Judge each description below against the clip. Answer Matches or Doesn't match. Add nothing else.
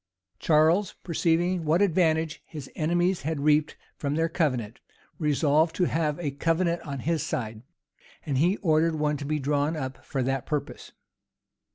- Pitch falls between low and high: Matches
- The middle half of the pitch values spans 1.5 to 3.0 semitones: Matches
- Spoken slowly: Doesn't match